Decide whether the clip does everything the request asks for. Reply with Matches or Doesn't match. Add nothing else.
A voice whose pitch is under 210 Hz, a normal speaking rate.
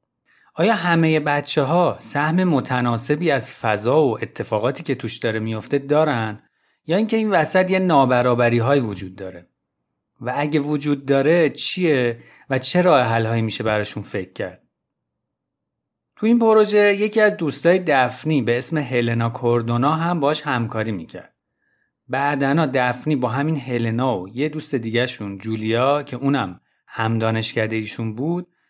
Matches